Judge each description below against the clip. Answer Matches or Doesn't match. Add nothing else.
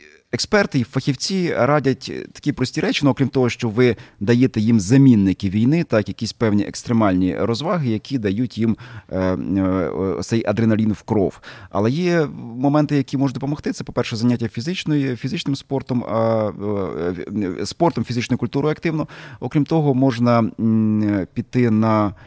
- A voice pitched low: Matches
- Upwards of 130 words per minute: Matches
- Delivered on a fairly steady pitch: Doesn't match